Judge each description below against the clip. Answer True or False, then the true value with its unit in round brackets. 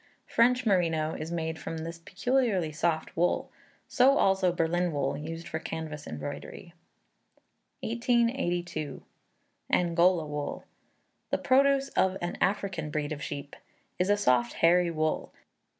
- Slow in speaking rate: True (125 wpm)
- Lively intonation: False (3.6 semitones)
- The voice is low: False (170 Hz)